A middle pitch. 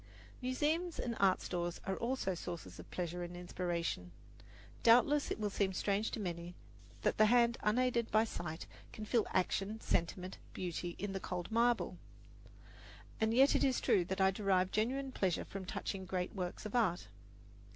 No: high, 195 Hz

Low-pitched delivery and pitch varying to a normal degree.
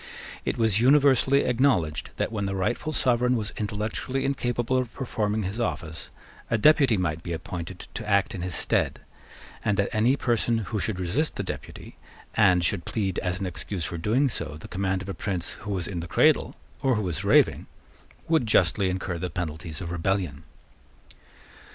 Yes: low, 100 Hz; average, 5.0 semitones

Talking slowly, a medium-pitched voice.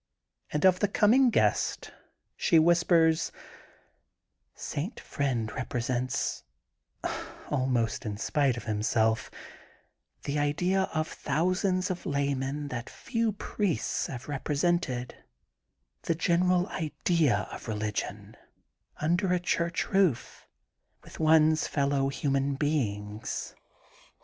Yes: slow, 105 wpm; medium, 145 Hz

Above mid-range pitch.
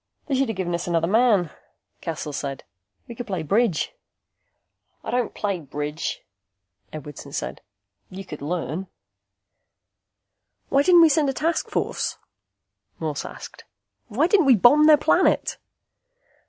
Yes: high, 195 Hz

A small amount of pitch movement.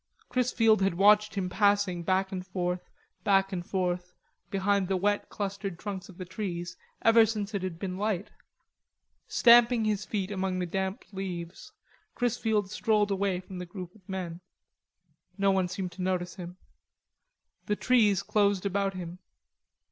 Yes: narrow, 2.2 semitones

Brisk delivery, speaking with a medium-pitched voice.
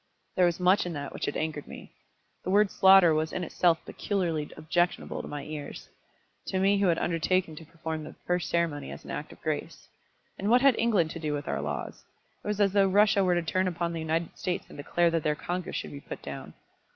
Yes: fast, 230 wpm; medium, 175 Hz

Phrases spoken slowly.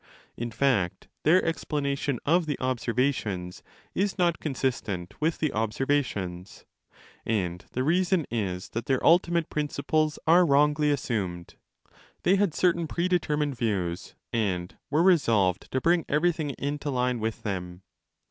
Yes: slow, 125 wpm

